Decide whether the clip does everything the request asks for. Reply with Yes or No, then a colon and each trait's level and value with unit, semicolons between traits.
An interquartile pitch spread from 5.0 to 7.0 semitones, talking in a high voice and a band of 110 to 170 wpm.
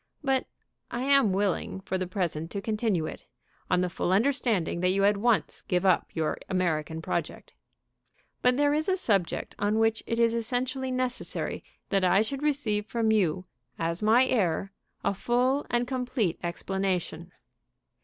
Yes: average, 5.3 semitones; high, 210 Hz; average, 160 wpm